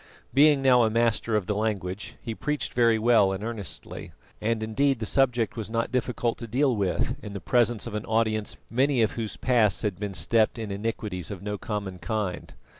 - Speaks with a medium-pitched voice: No, low, 110 Hz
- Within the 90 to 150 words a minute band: No, average, 195 wpm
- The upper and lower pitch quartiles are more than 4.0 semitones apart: No, narrow, 2.6 semitones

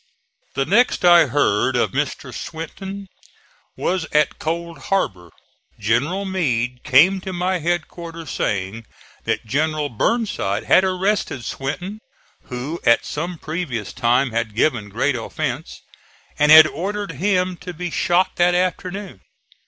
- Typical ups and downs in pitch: No, wide, 6.4 semitones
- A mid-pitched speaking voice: Yes, medium, 160 Hz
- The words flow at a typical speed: No, slow, 130 wpm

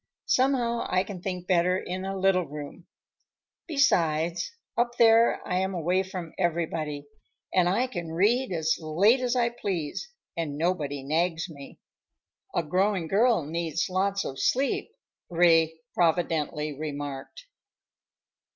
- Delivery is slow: Yes, slow, 130 wpm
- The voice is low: No, medium, 175 Hz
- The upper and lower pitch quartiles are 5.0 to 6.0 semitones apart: No, average, 3.7 semitones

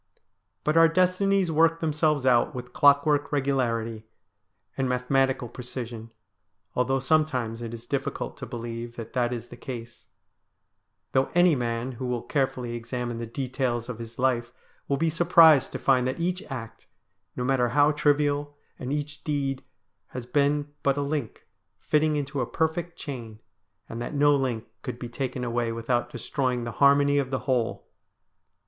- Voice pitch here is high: No, low, 130 Hz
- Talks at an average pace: Yes, average, 160 wpm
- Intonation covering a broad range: No, average, 3.3 semitones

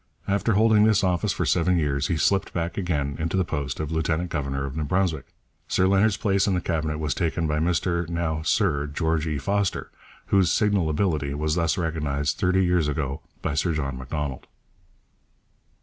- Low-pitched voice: Yes, very low, 80 Hz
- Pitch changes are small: No, average, 3.7 semitones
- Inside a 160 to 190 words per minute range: Yes, average, 180 wpm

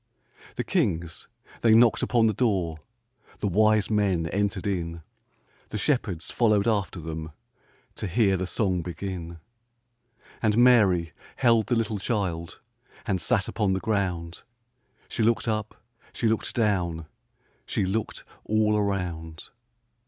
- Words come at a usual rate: No, slow, 130 wpm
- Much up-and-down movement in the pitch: No, average, 4.1 semitones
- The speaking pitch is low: Yes, low, 100 Hz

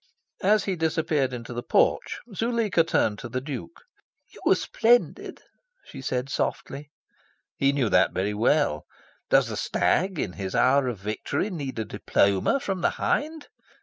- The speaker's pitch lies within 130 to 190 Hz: Yes, medium, 140 Hz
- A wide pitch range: Yes, wide, 7.9 semitones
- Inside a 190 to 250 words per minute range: No, average, 155 wpm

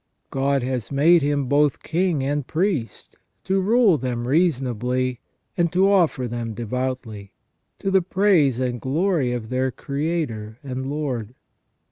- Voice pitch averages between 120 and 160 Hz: Yes, low, 135 Hz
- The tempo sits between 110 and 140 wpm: Yes, slow, 135 wpm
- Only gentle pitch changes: No, average, 5.3 semitones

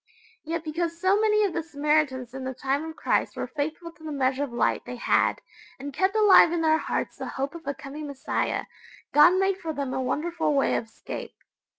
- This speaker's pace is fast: Yes, fast, 215 wpm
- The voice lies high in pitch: Yes, very high, 305 Hz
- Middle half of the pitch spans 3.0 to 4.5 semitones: Yes, average, 3.7 semitones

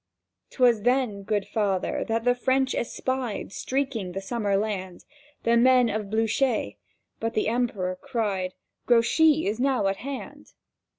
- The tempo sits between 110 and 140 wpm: Yes, slow, 135 wpm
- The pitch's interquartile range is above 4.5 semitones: No, average, 4.0 semitones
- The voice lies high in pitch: Yes, high, 230 Hz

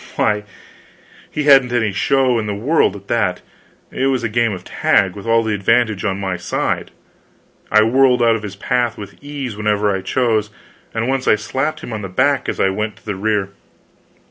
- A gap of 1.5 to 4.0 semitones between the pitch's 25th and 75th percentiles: Yes, average, 3.6 semitones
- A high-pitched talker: No, low, 110 Hz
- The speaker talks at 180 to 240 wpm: Yes, average, 200 wpm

